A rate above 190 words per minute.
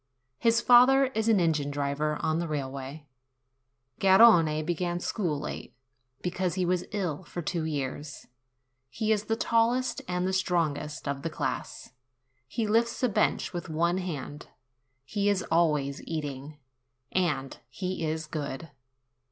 No: average, 140 wpm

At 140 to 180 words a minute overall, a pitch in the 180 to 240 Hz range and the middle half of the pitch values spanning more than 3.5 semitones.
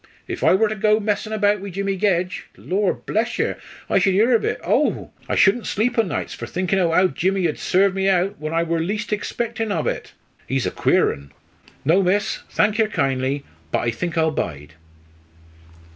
No: fast, 205 wpm; high, 190 Hz; average, 4.0 semitones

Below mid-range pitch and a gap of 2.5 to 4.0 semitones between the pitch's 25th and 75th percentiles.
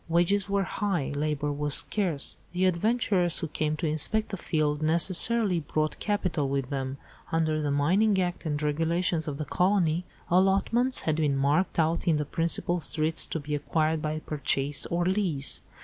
No: medium, 160 Hz; average, 3.6 semitones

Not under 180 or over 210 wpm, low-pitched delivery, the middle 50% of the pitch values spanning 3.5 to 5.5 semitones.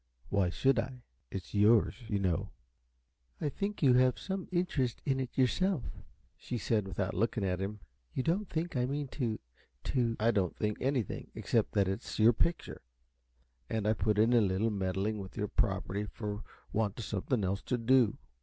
Yes: average, 185 wpm; low, 115 Hz; average, 4.3 semitones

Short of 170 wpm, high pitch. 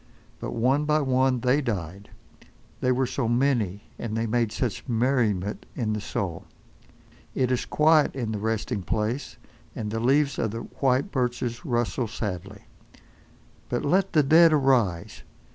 No: average, 150 wpm; low, 120 Hz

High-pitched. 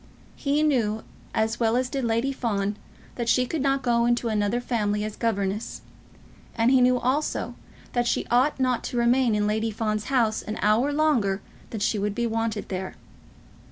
Yes: high, 230 Hz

